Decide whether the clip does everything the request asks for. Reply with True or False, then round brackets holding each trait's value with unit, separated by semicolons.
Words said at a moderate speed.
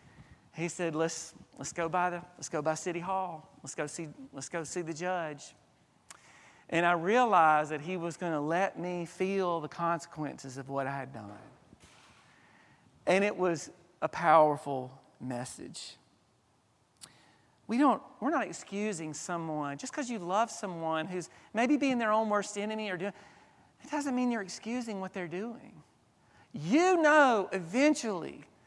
True (155 wpm)